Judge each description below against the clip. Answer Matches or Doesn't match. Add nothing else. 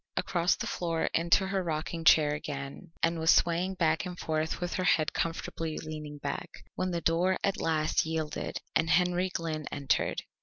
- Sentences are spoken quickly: Doesn't match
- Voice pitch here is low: Doesn't match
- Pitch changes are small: Matches